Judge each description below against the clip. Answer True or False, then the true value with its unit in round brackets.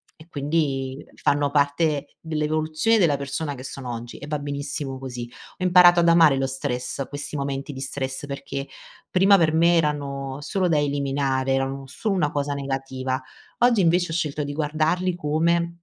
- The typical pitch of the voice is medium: True (145 Hz)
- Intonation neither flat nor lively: True (3.1 semitones)